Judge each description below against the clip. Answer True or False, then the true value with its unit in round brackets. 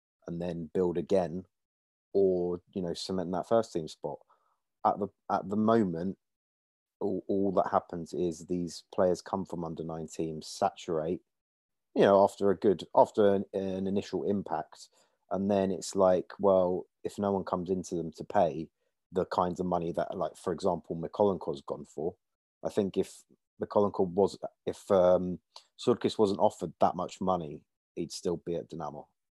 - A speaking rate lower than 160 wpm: False (170 wpm)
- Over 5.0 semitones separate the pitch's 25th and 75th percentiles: False (2.6 semitones)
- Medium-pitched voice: False (90 Hz)